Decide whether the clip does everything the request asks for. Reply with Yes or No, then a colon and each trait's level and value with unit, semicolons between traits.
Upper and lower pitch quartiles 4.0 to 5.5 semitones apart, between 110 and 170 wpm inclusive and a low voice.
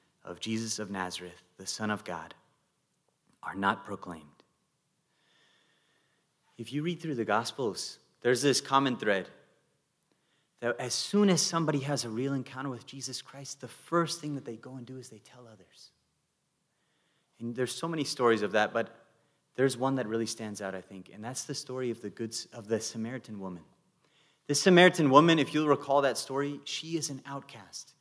No: average, 4.7 semitones; average, 180 wpm; low, 130 Hz